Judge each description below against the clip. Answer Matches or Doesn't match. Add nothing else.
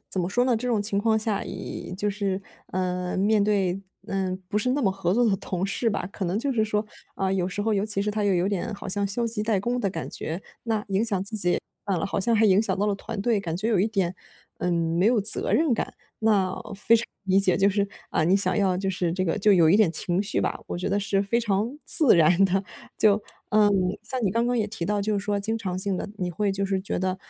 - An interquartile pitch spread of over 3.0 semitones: Doesn't match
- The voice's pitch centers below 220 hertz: Matches